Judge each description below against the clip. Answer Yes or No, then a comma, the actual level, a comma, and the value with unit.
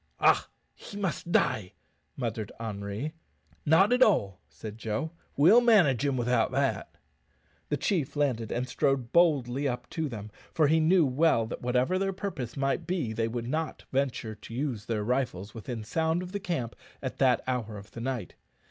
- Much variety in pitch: Yes, wide, 6.0 semitones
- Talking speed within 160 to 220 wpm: Yes, average, 175 wpm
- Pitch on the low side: Yes, low, 130 Hz